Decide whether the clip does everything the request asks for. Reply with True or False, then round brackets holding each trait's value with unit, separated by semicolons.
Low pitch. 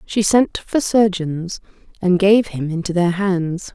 False (190 Hz)